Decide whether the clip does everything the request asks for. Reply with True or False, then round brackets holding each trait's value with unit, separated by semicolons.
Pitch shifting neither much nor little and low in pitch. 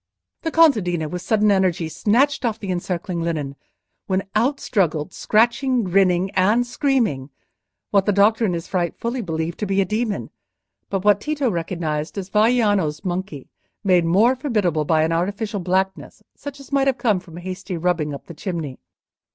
False (4.6 semitones; 190 Hz)